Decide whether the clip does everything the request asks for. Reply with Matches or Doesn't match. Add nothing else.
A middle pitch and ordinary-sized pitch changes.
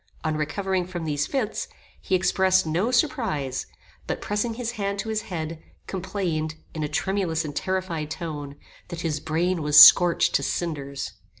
Matches